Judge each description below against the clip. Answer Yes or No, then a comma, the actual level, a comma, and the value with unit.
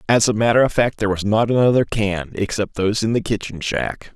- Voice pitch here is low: Yes, low, 110 Hz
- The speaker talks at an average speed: No, fast, 230 wpm